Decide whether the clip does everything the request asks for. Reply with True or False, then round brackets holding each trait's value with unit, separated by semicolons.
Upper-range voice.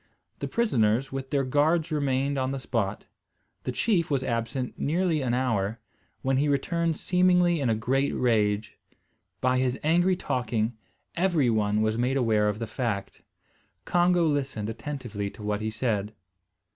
False (130 Hz)